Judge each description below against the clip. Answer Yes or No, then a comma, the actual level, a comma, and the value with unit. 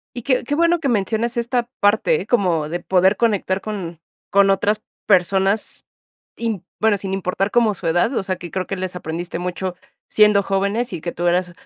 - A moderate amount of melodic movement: Yes, average, 3.6 semitones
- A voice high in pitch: Yes, high, 195 Hz